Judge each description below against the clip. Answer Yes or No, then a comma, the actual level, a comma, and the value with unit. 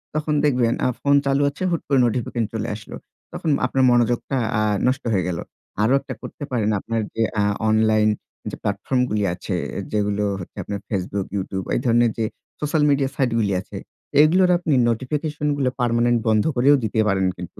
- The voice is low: Yes, low, 120 Hz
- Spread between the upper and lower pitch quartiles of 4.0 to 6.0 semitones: Yes, average, 4.5 semitones